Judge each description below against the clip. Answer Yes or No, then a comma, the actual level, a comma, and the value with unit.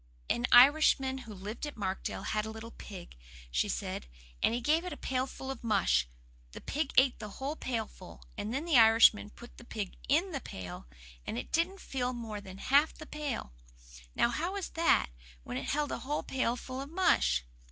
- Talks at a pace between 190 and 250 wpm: Yes, average, 195 wpm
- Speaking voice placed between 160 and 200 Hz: No, high, 245 Hz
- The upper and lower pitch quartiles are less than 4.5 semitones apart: No, wide, 5.6 semitones